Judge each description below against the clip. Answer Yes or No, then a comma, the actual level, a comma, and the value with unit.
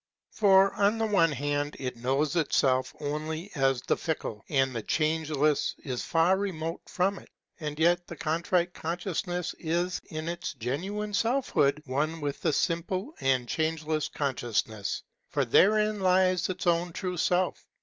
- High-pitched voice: No, medium, 160 Hz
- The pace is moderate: Yes, average, 150 wpm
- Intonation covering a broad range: No, average, 4.1 semitones